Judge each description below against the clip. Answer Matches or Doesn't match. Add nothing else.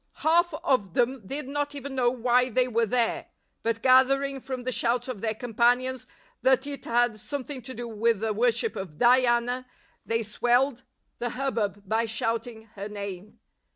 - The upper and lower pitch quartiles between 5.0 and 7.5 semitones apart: Doesn't match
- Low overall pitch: Doesn't match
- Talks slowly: Doesn't match